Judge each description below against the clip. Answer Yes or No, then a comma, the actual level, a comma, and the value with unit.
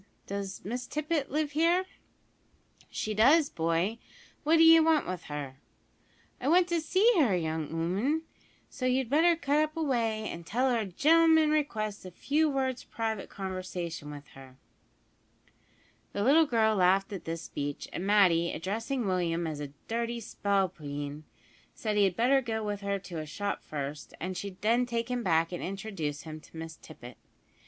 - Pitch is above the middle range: Yes, high, 210 Hz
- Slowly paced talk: No, average, 165 wpm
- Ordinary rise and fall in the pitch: No, wide, 8.1 semitones